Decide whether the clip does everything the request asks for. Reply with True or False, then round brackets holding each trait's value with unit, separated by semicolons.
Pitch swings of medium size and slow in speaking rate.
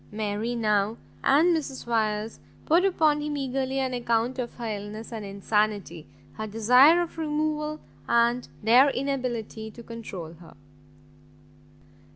True (4.3 semitones; 130 wpm)